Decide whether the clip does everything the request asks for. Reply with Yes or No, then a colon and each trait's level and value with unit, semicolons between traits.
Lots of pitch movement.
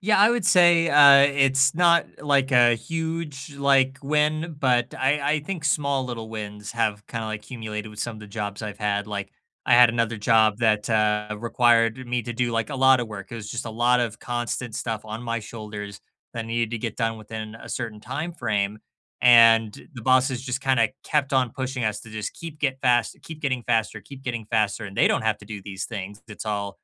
No: average, 3.8 semitones